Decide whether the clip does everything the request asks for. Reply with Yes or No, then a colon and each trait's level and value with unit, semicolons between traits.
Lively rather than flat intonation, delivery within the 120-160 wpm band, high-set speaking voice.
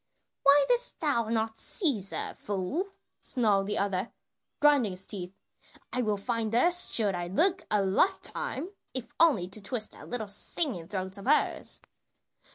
Yes: wide, 6.6 semitones; average, 155 wpm; high, 220 Hz